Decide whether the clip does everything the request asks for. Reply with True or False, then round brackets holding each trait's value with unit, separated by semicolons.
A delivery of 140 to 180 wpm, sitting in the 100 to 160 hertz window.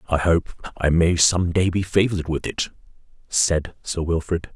False (170 wpm; 85 Hz)